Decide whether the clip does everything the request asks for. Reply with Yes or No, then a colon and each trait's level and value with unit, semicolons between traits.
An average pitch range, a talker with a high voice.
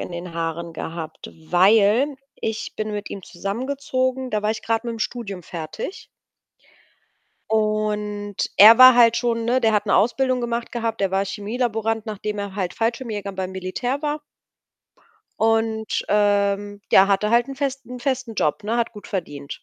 Yes: average, 3.1 semitones; high, 215 Hz